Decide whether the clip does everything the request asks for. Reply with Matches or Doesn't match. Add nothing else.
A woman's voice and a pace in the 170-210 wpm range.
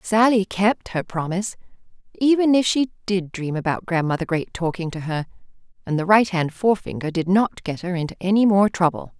Matches